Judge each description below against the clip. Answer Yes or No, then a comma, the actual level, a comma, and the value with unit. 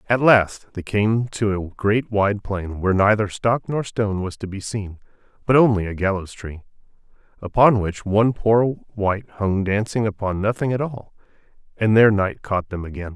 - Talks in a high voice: No, low, 105 Hz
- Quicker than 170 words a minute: Yes, average, 180 wpm